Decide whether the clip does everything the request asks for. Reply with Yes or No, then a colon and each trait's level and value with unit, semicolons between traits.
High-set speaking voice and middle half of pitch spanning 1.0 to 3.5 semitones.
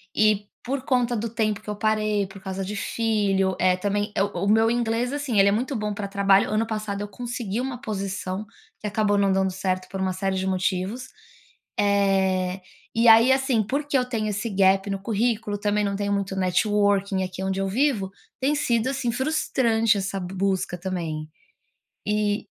Yes: high, 205 Hz; average, 2.8 semitones